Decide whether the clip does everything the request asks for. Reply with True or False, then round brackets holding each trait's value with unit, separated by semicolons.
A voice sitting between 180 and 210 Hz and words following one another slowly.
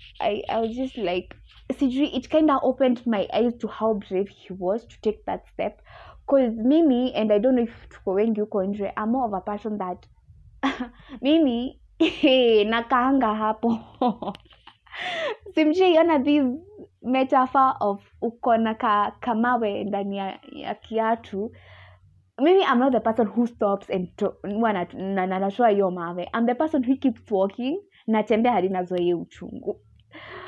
False (230 Hz; 130 wpm)